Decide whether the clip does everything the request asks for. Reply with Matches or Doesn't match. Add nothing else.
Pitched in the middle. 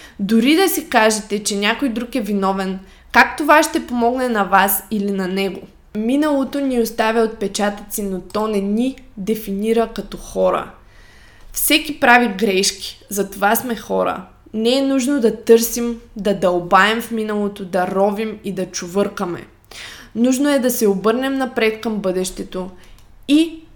Doesn't match